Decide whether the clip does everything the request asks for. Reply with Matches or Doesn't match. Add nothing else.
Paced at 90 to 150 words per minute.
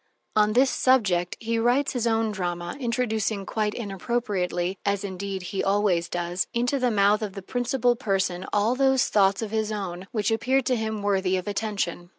Doesn't match